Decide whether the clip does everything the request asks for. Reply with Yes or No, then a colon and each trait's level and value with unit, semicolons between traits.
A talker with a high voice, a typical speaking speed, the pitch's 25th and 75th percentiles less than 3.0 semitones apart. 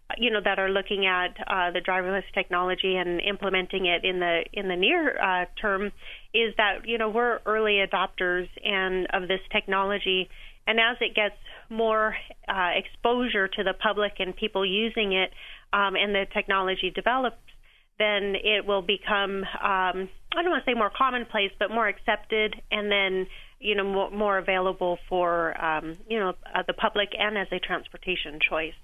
Yes: high, 195 Hz; average, 175 wpm; narrow, 2.4 semitones